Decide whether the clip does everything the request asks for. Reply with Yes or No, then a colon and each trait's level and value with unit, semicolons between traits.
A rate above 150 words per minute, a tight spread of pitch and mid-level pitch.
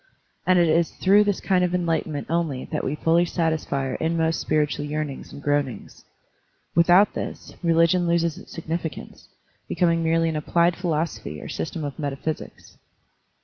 Yes: average, 160 wpm; narrow, 2.1 semitones; medium, 165 Hz